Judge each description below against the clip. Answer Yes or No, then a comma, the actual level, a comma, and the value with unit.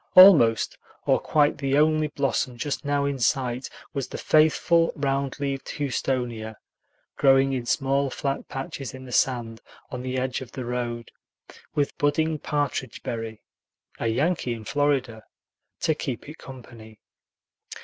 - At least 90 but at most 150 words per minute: Yes, average, 140 wpm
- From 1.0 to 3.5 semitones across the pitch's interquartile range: Yes, average, 2.9 semitones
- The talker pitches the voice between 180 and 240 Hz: No, low, 135 Hz